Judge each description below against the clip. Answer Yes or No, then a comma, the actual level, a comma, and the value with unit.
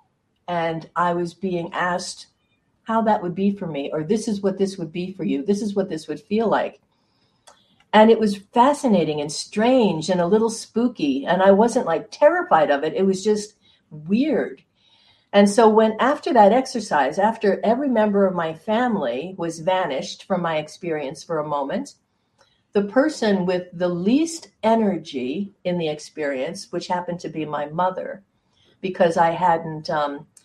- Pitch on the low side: No, high, 190 Hz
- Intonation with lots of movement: No, average, 4.5 semitones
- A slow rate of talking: No, average, 170 wpm